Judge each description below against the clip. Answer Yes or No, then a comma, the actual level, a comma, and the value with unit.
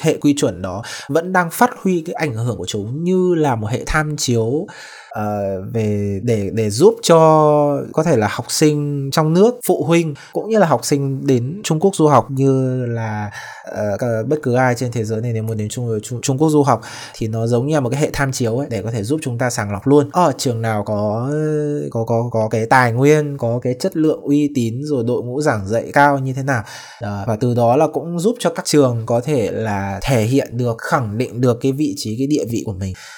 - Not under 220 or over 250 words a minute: Yes, average, 245 wpm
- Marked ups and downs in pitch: No, average, 4.9 semitones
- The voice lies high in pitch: No, low, 130 Hz